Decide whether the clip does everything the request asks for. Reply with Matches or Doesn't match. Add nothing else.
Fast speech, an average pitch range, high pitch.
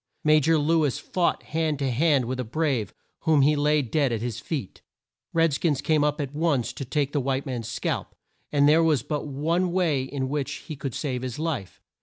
Doesn't match